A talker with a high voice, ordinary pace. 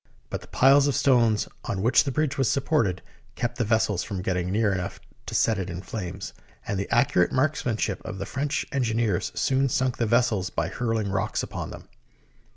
No: low, 115 Hz; average, 195 wpm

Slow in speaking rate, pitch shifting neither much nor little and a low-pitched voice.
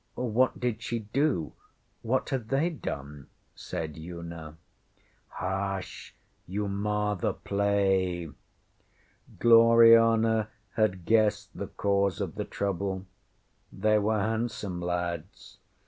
Yes: slow, 100 wpm; average, 3.8 semitones; low, 100 Hz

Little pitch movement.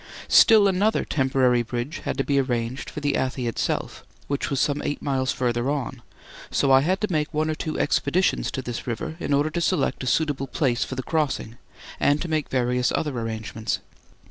No: average, 3.7 semitones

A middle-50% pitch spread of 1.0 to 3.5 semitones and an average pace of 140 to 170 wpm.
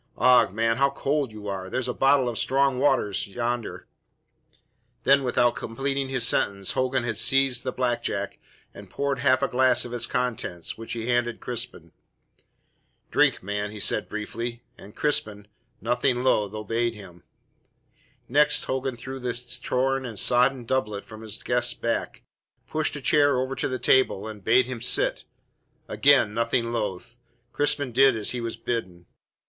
Yes: average, 2.9 semitones; average, 165 wpm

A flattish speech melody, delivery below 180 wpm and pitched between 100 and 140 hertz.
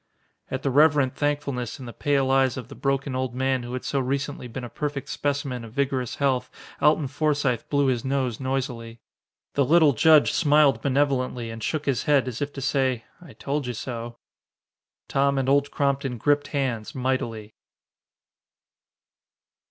Yes: narrow, 2.3 semitones; average, 165 wpm; low, 135 Hz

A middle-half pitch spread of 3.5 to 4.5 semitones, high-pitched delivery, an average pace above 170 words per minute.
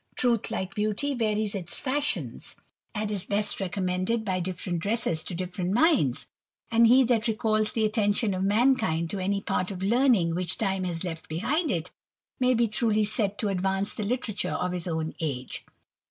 Yes: average, 3.8 semitones; high, 205 Hz; average, 180 wpm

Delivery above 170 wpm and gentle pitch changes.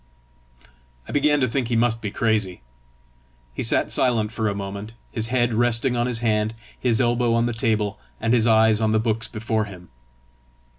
Yes: average, 185 wpm; narrow, 1.8 semitones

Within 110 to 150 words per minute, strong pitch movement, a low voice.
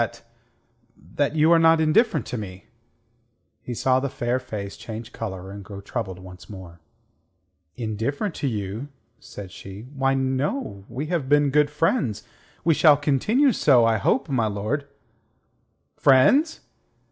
Yes: average, 145 wpm; wide, 6.3 semitones; low, 130 Hz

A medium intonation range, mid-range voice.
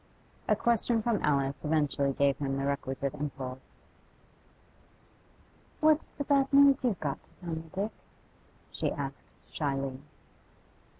No: wide, 8.5 semitones; medium, 150 Hz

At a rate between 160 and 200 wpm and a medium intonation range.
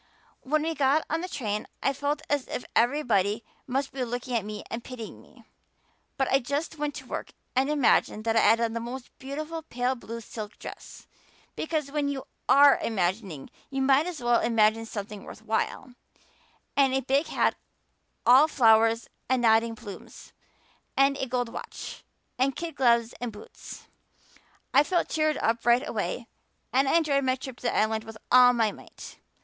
Yes: average, 175 wpm; average, 3.7 semitones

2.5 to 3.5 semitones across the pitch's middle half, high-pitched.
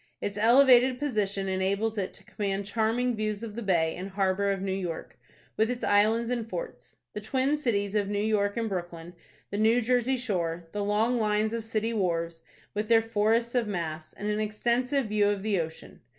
Yes: average, 2.9 semitones; high, 210 Hz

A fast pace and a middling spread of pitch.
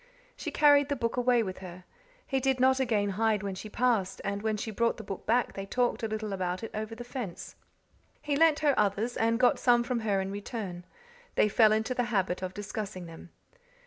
Yes: fast, 215 wpm; average, 3.8 semitones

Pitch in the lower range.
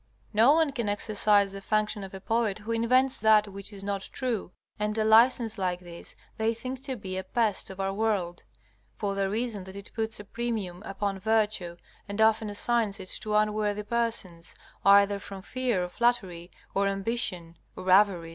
No: high, 210 Hz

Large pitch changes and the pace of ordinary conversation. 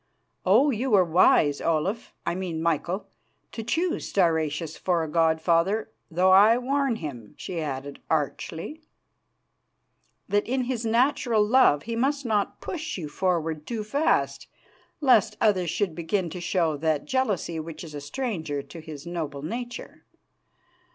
Yes: wide, 6.3 semitones; average, 145 wpm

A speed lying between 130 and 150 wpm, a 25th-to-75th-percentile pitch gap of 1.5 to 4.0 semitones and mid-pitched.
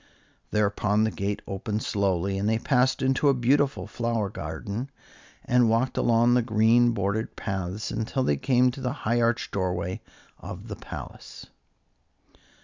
No: average, 145 wpm; average, 3.7 semitones; low, 110 Hz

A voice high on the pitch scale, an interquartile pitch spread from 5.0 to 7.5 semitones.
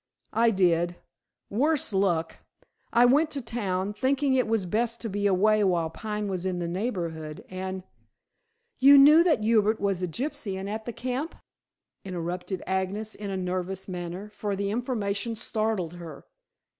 No: high, 205 Hz; average, 4.3 semitones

